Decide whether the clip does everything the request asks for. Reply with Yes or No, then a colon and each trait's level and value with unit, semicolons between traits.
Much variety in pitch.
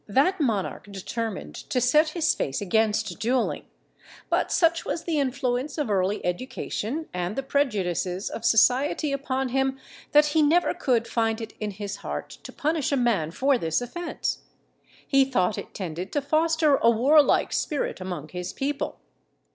Yes: wide, 6.1 semitones